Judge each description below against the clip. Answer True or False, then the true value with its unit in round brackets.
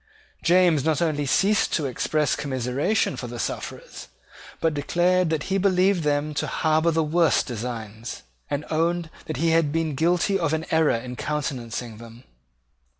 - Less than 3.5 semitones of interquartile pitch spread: False (3.9 semitones)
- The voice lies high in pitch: False (155 Hz)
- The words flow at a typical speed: True (155 wpm)